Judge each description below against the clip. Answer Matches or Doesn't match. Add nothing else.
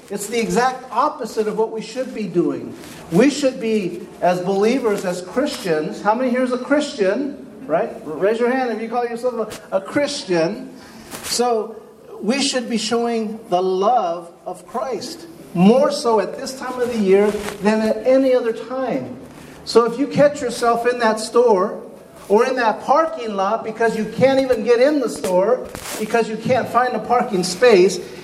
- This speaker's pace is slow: Doesn't match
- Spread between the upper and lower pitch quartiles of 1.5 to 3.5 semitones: Matches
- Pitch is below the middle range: Doesn't match